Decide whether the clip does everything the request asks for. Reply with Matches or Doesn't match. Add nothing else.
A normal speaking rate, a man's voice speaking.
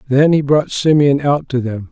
Doesn't match